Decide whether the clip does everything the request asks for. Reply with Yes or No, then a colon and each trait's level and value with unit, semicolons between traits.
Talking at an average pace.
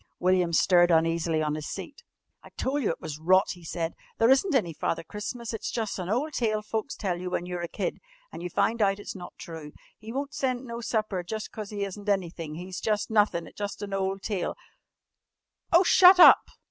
No: fast, 210 wpm